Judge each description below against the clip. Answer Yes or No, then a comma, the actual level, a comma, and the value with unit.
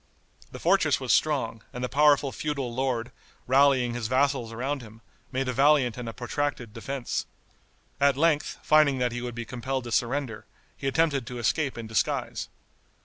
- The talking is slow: No, average, 170 wpm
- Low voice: Yes, low, 130 Hz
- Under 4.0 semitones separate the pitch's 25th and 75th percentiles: Yes, average, 2.9 semitones